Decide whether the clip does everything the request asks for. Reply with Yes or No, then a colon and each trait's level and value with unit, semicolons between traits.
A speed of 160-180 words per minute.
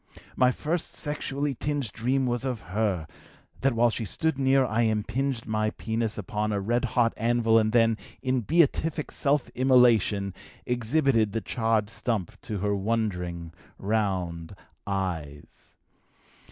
No: slow, 135 wpm